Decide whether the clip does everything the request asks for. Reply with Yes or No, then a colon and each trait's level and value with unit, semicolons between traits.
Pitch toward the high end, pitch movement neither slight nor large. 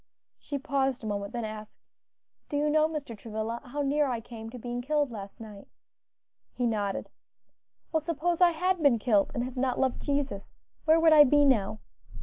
Yes: very high, 255 Hz; average, 5.0 semitones